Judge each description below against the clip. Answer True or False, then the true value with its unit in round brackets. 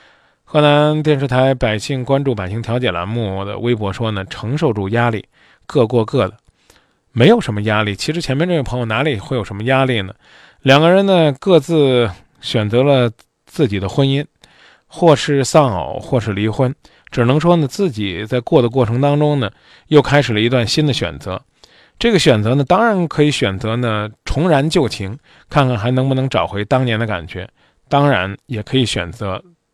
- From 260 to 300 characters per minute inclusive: True (270 characters per minute)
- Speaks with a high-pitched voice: False (125 Hz)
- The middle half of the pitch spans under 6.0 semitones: True (5.1 semitones)